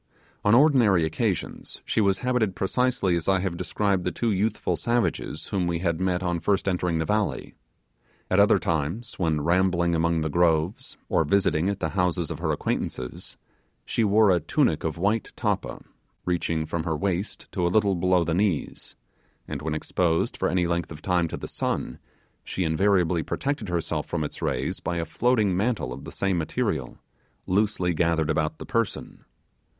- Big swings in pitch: No, average, 3.4 semitones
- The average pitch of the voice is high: No, very low, 90 Hz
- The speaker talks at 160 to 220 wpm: Yes, average, 175 wpm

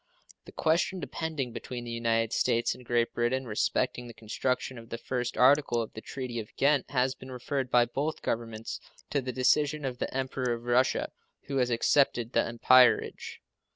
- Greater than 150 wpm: Yes, average, 180 wpm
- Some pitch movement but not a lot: No, narrow, 2.1 semitones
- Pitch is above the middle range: No, low, 125 Hz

